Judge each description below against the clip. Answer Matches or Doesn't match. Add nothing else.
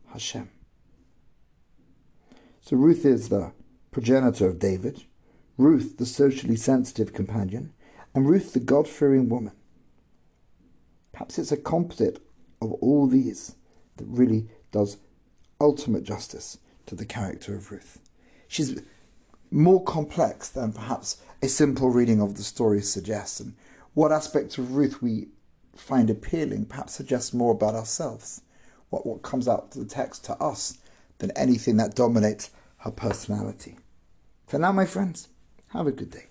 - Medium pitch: Doesn't match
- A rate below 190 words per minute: Matches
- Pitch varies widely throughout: Doesn't match